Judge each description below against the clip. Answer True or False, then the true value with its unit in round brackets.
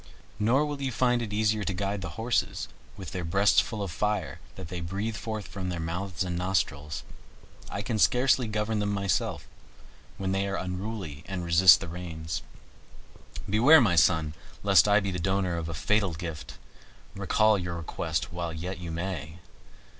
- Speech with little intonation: False (3.9 semitones)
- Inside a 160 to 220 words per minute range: True (175 wpm)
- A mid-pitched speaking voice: False (95 Hz)